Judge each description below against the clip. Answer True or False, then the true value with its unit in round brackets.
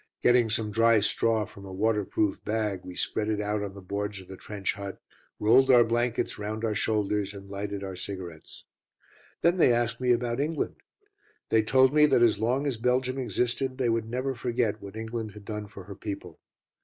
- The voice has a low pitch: True (110 Hz)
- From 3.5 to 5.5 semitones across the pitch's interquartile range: False (3.1 semitones)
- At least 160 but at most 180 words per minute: False (195 wpm)